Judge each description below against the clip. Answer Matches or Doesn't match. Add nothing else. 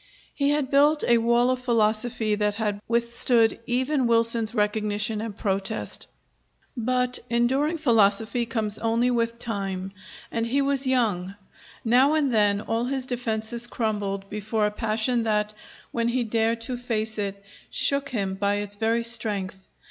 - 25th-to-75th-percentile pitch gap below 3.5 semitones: Matches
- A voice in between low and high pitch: Doesn't match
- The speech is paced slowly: Doesn't match